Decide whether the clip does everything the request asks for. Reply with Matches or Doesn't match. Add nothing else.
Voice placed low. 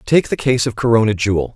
Matches